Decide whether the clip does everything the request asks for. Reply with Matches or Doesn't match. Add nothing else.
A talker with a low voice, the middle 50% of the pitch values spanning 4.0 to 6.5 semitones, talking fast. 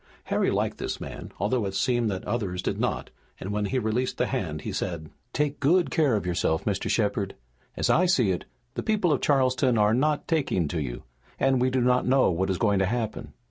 Matches